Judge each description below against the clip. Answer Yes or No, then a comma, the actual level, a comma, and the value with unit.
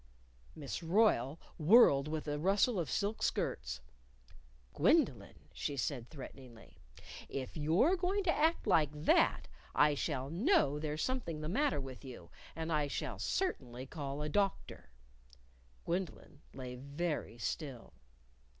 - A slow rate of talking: Yes, slow, 130 wpm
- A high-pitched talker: No, medium, 150 Hz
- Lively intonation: Yes, wide, 6.0 semitones